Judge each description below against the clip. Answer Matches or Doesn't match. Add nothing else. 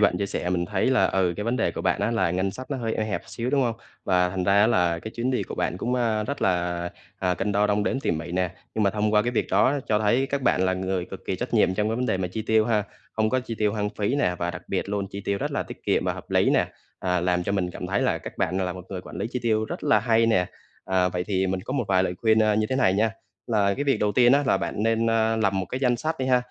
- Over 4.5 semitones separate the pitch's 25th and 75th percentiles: Doesn't match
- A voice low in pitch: Matches